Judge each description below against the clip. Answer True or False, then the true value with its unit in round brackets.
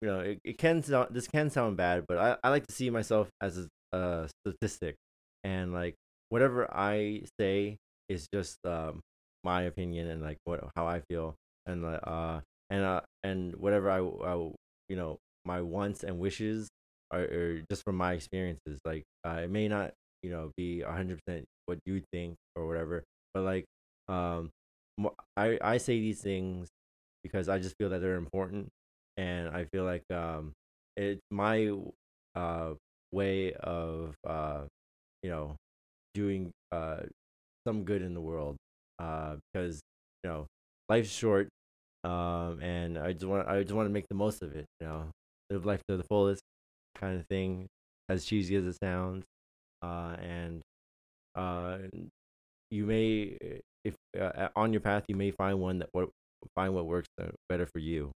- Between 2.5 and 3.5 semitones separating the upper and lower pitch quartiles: False (4.3 semitones)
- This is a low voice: True (90 Hz)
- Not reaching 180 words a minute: True (170 wpm)